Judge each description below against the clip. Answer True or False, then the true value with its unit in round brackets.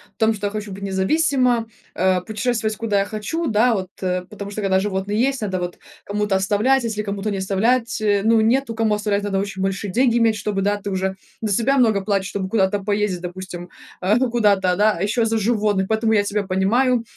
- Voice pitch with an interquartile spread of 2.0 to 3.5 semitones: True (2.7 semitones)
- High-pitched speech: True (210 Hz)